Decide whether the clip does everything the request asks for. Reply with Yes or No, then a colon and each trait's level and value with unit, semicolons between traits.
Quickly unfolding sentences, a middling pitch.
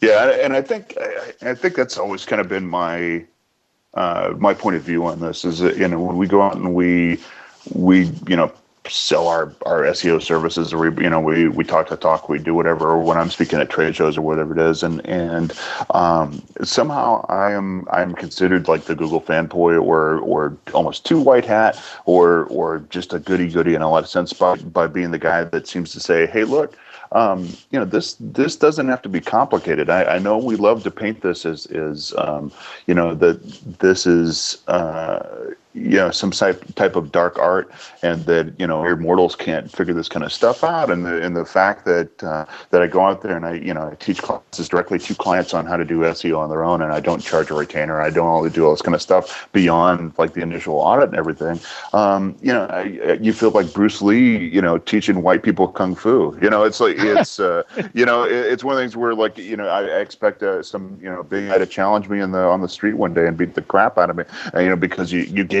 No: fast, 240 wpm; very low, 90 Hz